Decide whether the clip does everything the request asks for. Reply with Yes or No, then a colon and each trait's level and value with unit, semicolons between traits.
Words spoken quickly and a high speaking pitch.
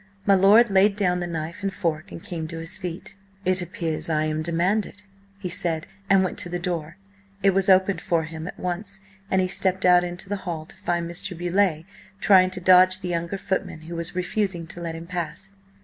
No: fast, 210 wpm; medium, 180 Hz